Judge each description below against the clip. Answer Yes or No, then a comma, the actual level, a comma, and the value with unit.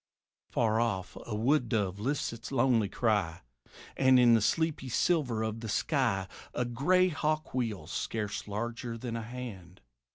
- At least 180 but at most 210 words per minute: No, average, 155 wpm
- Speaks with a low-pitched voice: Yes, low, 115 Hz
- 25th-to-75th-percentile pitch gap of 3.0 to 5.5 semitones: Yes, average, 3.4 semitones